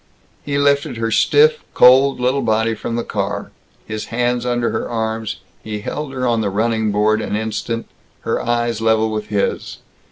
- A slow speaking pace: No, average, 170 wpm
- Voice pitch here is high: No, low, 115 Hz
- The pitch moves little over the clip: Yes, narrow, 2.2 semitones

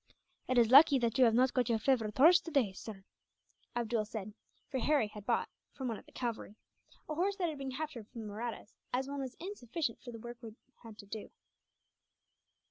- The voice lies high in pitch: Yes, high, 240 Hz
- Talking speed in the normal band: No, fast, 210 wpm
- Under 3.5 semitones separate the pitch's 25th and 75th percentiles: No, average, 3.9 semitones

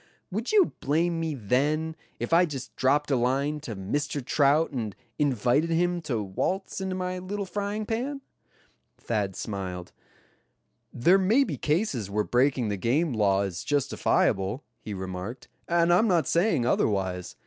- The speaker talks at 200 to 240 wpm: No, average, 150 wpm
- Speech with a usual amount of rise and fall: No, wide, 8.3 semitones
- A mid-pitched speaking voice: Yes, medium, 145 Hz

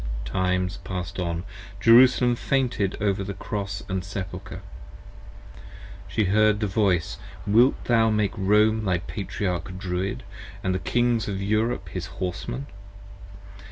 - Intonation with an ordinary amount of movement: Yes, average, 3.0 semitones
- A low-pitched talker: Yes, low, 100 Hz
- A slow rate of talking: Yes, slow, 125 wpm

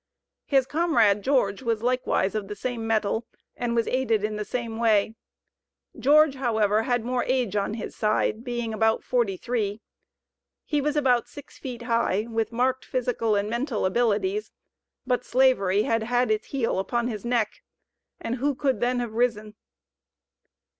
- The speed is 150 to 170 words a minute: Yes, average, 160 wpm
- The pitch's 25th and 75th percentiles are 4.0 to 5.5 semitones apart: No, average, 2.8 semitones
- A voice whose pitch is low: No, high, 235 Hz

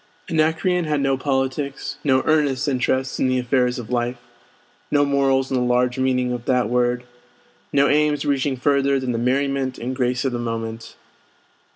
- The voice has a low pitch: Yes, low, 130 Hz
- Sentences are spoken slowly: No, average, 170 wpm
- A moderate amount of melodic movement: No, narrow, 2.0 semitones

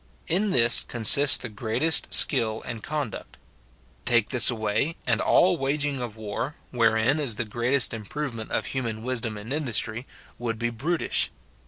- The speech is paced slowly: No, average, 155 wpm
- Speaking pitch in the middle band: No, low, 120 Hz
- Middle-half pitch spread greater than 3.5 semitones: Yes, average, 3.9 semitones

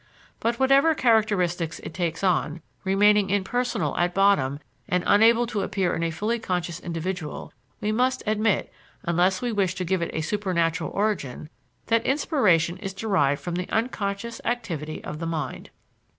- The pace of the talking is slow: No, average, 155 wpm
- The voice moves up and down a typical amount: Yes, average, 4.6 semitones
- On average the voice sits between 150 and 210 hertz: Yes, high, 190 Hz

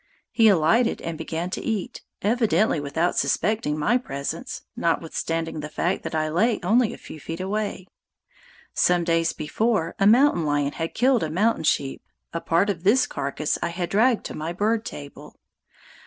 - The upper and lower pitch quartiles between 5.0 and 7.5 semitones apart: Yes, average, 5.3 semitones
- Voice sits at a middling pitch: Yes, medium, 175 Hz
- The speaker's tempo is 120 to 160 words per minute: No, average, 170 wpm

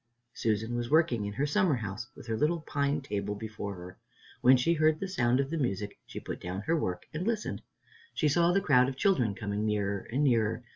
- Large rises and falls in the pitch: Yes, wide, 6.7 semitones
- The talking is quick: Yes, fast, 220 wpm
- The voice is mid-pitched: No, low, 125 Hz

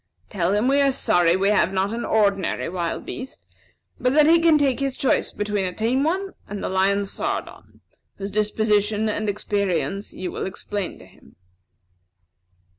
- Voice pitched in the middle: No, high, 210 Hz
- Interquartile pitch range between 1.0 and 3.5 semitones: No, average, 4.6 semitones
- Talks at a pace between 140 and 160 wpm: No, average, 170 wpm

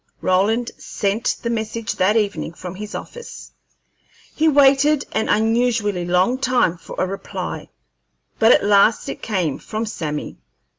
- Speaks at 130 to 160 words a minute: Yes, average, 140 wpm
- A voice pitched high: Yes, high, 220 Hz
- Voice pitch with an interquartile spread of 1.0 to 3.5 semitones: No, average, 4.1 semitones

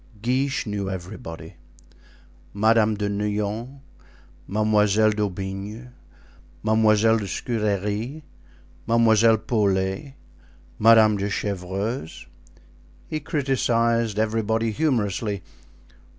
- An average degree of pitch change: No, narrow, 2.2 semitones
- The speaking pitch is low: Yes, low, 110 Hz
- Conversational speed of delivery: No, slow, 70 wpm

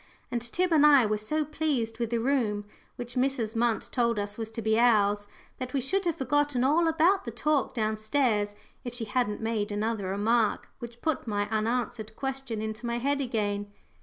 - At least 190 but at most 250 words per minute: Yes, average, 195 wpm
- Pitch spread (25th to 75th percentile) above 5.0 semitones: No, average, 3.8 semitones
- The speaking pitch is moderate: No, high, 235 Hz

